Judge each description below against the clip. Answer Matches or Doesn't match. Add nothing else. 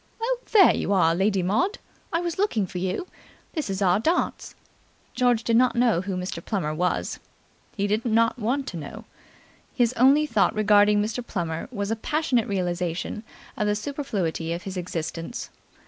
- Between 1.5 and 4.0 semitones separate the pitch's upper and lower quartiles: Doesn't match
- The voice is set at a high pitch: Matches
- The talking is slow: Doesn't match